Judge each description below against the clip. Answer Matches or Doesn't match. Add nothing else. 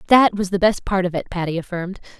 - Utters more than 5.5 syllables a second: Matches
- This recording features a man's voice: Doesn't match